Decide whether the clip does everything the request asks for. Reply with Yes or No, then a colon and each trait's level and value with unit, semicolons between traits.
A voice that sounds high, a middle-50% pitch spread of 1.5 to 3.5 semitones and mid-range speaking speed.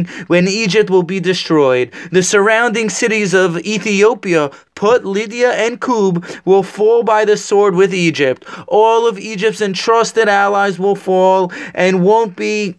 Yes: high, 200 Hz; average, 2.8 semitones; average, 145 wpm